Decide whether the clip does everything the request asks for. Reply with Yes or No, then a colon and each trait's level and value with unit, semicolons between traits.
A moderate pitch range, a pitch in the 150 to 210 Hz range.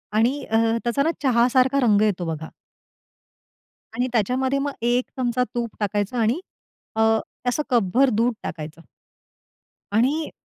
No: average, 3.4 semitones; high, 240 Hz